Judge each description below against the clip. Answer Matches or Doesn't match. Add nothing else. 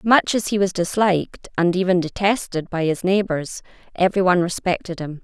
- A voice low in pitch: Doesn't match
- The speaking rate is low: Doesn't match